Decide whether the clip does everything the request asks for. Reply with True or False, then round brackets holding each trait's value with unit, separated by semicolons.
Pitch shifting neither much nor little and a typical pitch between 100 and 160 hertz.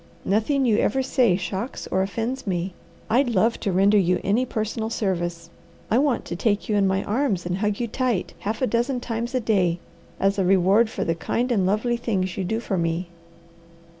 False (4.0 semitones; 210 Hz)